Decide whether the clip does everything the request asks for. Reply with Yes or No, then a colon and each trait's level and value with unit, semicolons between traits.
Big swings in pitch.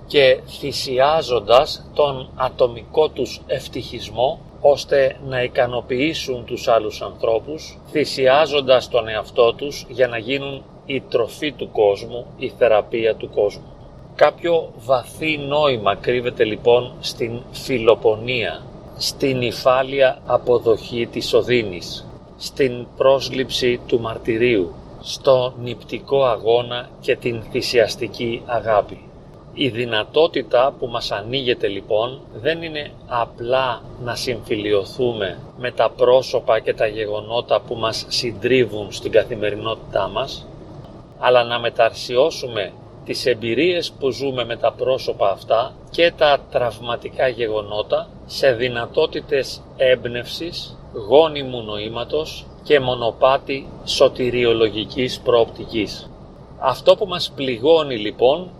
No: average, 4.5 semitones